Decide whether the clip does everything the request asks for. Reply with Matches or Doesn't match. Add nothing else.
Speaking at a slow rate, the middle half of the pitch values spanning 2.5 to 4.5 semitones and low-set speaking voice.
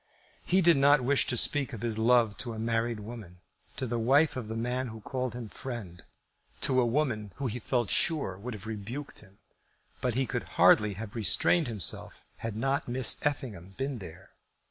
Doesn't match